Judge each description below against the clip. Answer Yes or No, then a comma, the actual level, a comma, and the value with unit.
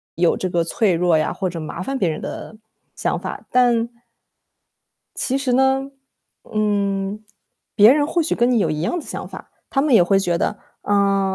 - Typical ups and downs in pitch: No, wide, 5.9 semitones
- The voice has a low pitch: No, high, 205 Hz